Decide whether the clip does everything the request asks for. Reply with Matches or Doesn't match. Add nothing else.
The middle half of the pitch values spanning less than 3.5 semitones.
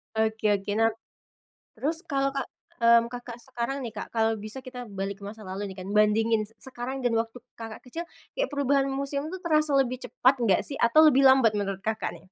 Doesn't match